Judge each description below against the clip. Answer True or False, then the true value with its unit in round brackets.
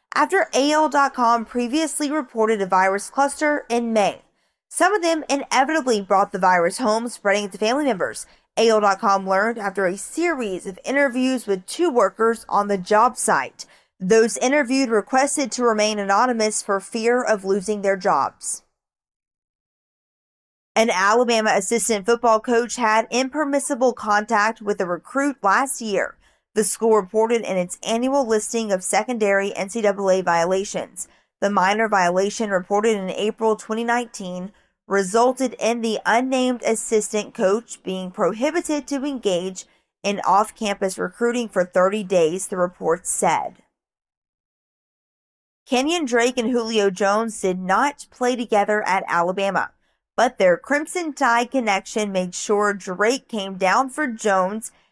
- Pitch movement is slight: False (4.0 semitones)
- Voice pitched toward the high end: True (220 Hz)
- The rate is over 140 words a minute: False (135 wpm)